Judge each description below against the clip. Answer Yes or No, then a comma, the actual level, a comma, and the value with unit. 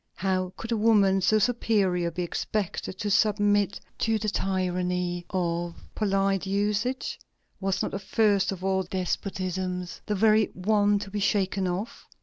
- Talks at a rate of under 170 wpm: Yes, average, 145 wpm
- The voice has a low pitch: No, high, 195 Hz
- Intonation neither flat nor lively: No, narrow, 2.1 semitones